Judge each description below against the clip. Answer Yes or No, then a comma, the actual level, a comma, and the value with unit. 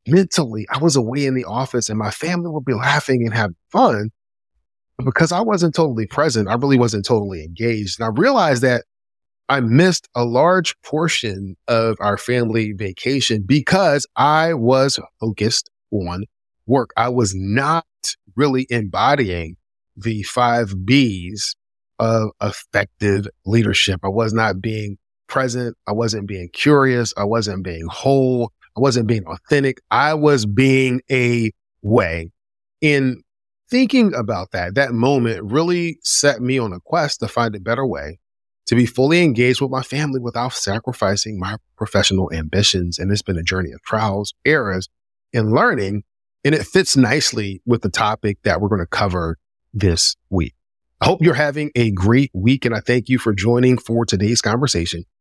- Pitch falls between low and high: No, low, 115 Hz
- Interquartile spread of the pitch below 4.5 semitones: No, average, 4.9 semitones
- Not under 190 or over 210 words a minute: No, average, 160 wpm